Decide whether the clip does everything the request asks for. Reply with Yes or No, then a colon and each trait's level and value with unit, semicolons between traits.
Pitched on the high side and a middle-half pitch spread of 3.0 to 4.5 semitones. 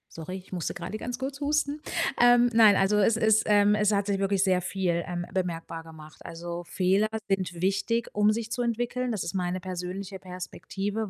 Yes: high, 195 Hz; average, 3.4 semitones